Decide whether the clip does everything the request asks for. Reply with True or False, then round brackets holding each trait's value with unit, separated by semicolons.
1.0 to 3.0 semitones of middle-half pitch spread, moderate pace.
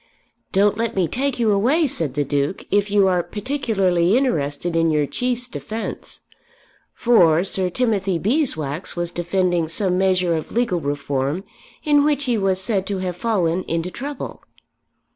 False (5.5 semitones; 155 wpm)